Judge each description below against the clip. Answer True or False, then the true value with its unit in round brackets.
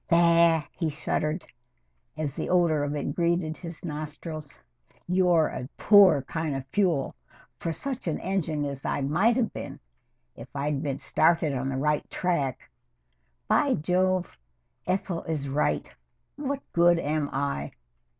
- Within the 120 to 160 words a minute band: True (140 wpm)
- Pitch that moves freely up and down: False (3.5 semitones)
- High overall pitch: False (160 Hz)